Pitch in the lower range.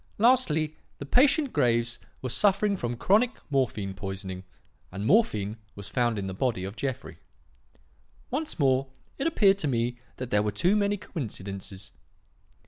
Yes: low, 125 Hz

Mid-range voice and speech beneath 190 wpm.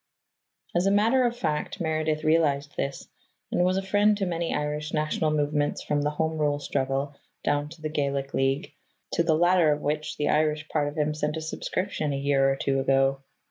No: medium, 150 Hz; average, 200 wpm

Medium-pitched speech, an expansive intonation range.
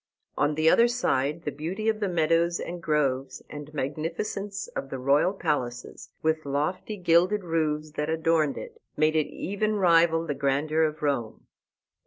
No: medium, 160 Hz; average, 3.3 semitones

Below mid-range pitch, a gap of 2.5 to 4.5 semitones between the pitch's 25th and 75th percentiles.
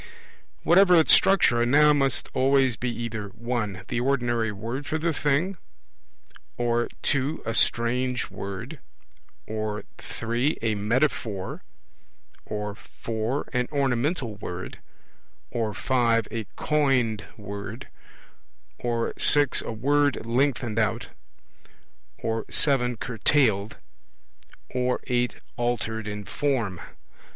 Yes: low, 120 Hz; average, 3.8 semitones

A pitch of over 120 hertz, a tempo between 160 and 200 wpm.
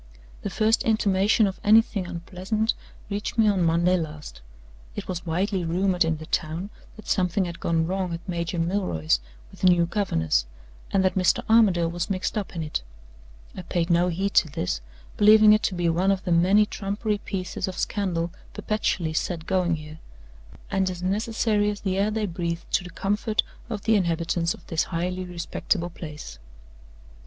Yes: medium, 185 Hz; average, 175 wpm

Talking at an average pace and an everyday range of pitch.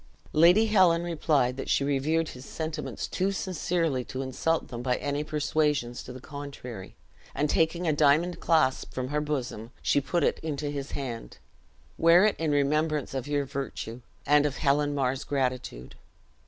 Yes: average, 165 wpm; average, 3.4 semitones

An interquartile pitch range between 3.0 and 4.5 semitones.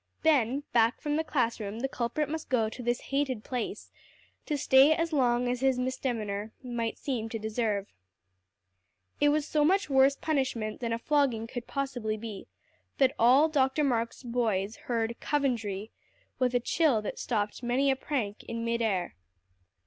Yes: average, 3.5 semitones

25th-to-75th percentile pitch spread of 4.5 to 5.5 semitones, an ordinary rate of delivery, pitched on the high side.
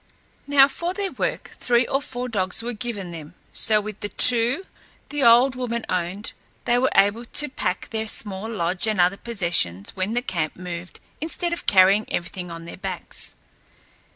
Yes: average, 5.1 semitones; average, 175 wpm; high, 215 Hz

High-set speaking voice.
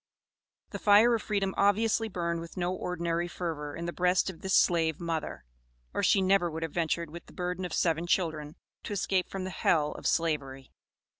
No: medium, 175 Hz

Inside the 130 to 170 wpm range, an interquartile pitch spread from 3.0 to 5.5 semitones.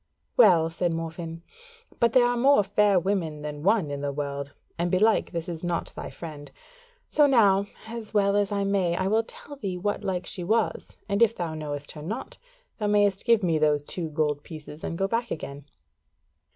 No: average, 195 wpm; average, 4.7 semitones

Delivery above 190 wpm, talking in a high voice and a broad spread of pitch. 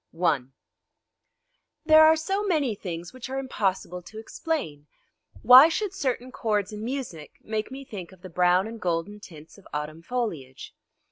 No: average, 155 wpm; high, 215 Hz; wide, 7.1 semitones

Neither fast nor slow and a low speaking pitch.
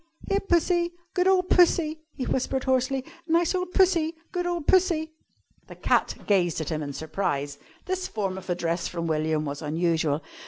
No: average, 165 wpm; very high, 260 Hz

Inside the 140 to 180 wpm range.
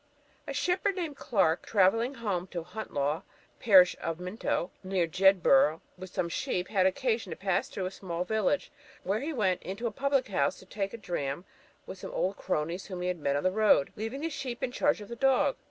No: fast, 205 wpm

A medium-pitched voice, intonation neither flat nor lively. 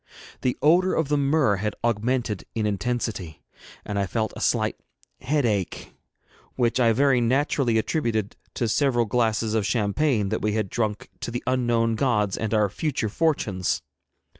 No: low, 115 Hz; average, 3.4 semitones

